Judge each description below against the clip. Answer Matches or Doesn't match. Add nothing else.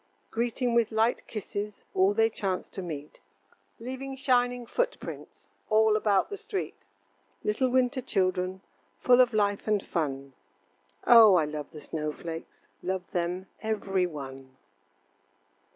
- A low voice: Doesn't match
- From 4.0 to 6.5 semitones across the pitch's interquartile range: Matches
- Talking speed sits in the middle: Doesn't match